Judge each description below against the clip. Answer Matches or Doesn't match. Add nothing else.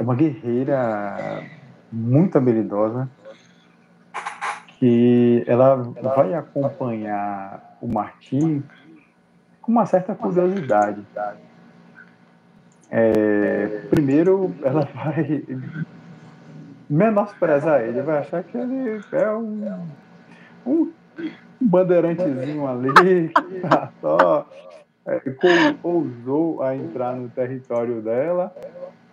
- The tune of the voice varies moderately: Doesn't match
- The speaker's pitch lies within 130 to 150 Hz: Matches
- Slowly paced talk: Matches